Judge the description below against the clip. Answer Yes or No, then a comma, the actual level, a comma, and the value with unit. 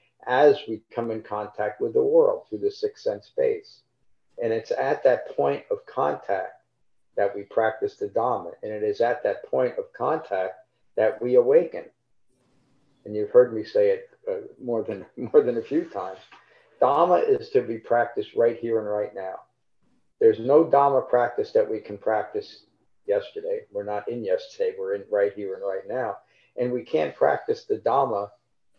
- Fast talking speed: No, average, 180 wpm